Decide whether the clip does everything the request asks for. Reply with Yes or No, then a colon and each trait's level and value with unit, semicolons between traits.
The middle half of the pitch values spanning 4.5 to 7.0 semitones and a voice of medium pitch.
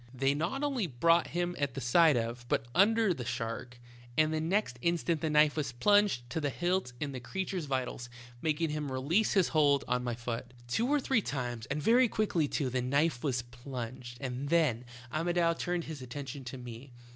Yes: wide, 5.5 semitones; medium, 145 Hz